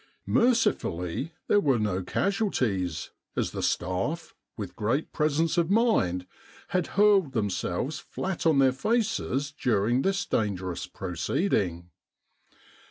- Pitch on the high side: No, low, 135 Hz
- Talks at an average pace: No, slow, 110 wpm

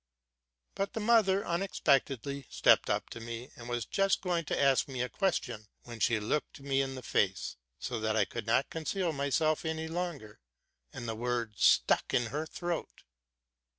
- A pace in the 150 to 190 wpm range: Yes, average, 180 wpm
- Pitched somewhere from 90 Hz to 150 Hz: Yes, low, 135 Hz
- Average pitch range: No, wide, 6.0 semitones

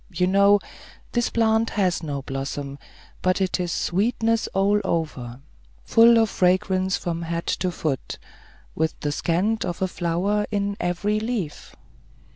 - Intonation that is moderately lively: Yes, average, 3.9 semitones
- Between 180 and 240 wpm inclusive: No, average, 140 wpm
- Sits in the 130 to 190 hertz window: Yes, medium, 185 Hz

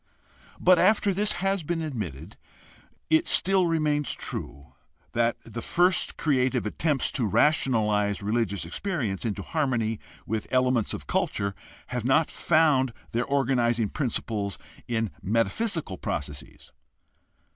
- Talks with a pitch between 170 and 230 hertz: No, low, 125 Hz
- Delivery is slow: Yes, slow, 115 wpm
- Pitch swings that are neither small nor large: No, wide, 6.8 semitones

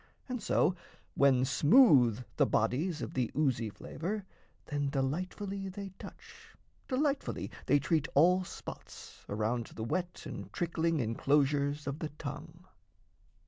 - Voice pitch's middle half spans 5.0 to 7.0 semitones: Yes, wide, 5.5 semitones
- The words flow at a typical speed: No, slow, 125 wpm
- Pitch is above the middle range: No, medium, 150 Hz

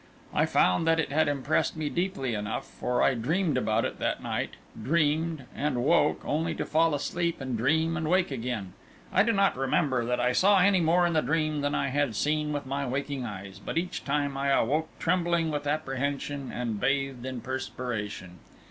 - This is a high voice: No, medium, 145 Hz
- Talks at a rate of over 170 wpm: Yes, average, 190 wpm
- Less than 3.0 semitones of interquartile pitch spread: No, average, 4.3 semitones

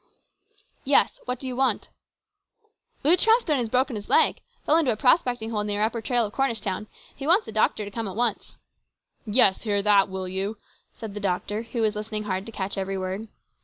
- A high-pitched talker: Yes, high, 220 Hz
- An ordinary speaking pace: No, fast, 225 wpm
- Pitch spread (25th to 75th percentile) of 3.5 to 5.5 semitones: Yes, average, 4.2 semitones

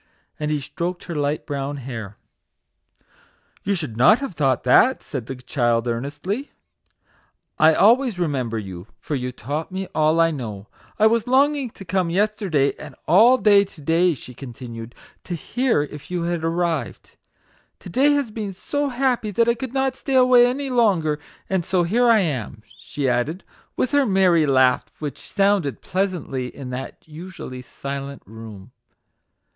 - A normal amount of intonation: No, wide, 8.0 semitones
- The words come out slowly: No, average, 170 wpm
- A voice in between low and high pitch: Yes, medium, 165 Hz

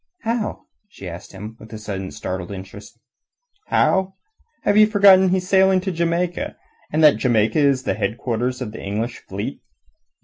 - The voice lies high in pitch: No, low, 125 Hz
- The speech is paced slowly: No, average, 165 wpm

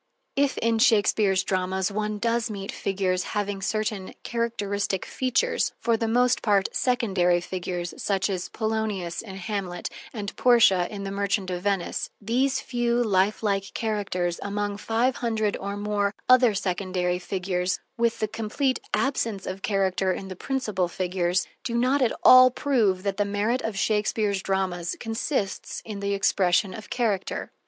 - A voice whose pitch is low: No, high, 205 Hz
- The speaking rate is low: No, average, 150 wpm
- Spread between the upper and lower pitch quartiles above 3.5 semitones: No, average, 3.1 semitones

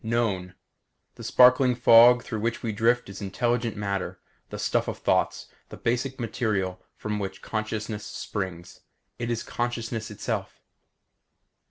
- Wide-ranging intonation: No, average, 2.8 semitones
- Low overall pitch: Yes, low, 110 Hz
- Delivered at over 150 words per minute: No, slow, 135 wpm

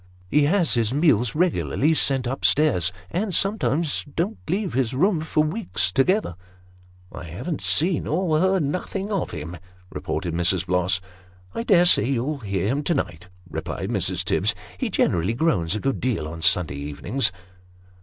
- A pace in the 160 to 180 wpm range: Yes, average, 165 wpm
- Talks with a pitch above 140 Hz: No, low, 135 Hz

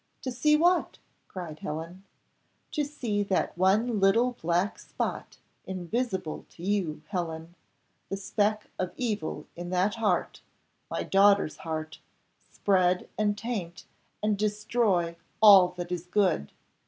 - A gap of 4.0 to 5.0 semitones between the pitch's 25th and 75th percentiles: No, average, 3.4 semitones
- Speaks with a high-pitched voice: Yes, high, 195 Hz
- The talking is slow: Yes, slow, 125 wpm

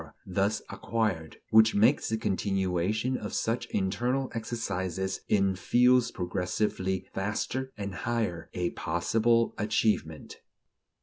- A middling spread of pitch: Yes, average, 3.5 semitones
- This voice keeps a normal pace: No, slow, 105 wpm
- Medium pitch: No, low, 105 Hz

